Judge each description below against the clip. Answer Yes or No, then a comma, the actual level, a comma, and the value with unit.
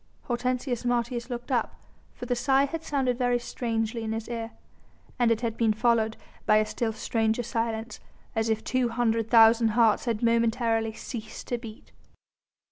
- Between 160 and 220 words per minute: Yes, average, 165 wpm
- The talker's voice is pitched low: No, high, 230 Hz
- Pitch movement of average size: No, narrow, 1.6 semitones